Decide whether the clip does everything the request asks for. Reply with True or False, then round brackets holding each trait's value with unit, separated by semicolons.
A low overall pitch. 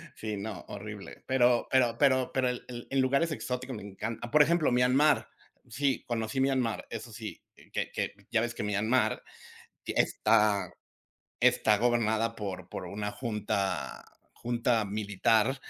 True (115 Hz)